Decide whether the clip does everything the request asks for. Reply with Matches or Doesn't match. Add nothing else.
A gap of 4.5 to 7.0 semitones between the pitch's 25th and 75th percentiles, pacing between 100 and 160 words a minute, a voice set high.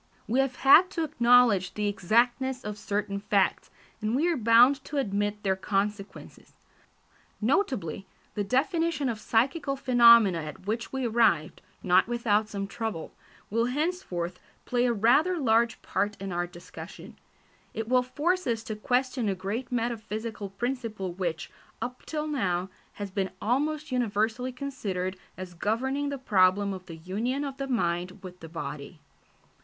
Matches